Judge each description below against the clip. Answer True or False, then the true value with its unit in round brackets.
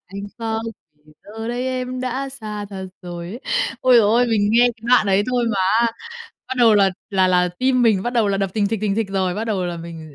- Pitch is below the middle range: False (215 Hz)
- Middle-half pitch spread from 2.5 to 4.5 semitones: True (4.0 semitones)